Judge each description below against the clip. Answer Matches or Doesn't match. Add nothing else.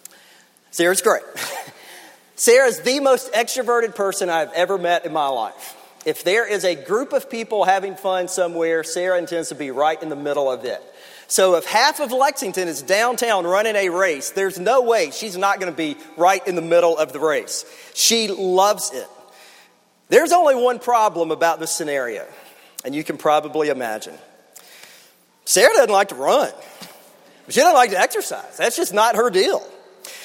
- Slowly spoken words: Doesn't match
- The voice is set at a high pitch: Matches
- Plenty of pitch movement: Matches